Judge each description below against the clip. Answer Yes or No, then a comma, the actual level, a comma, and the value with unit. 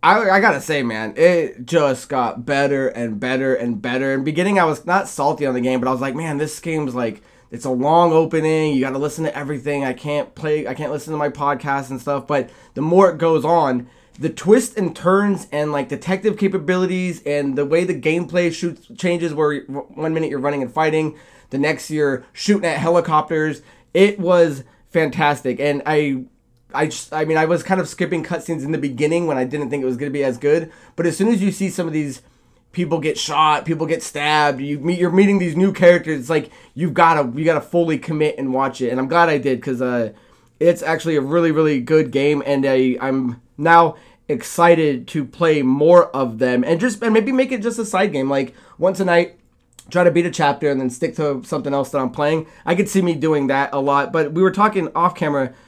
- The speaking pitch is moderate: Yes, medium, 155 Hz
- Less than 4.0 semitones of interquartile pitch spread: Yes, average, 3.6 semitones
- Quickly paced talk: Yes, fast, 230 wpm